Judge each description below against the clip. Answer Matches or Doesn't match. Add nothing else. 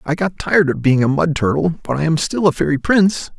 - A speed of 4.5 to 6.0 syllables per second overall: Matches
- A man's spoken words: Matches